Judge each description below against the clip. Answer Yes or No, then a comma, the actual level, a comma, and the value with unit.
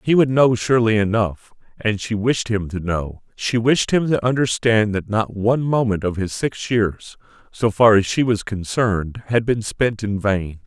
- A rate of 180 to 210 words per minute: Yes, average, 195 wpm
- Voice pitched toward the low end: Yes, low, 110 Hz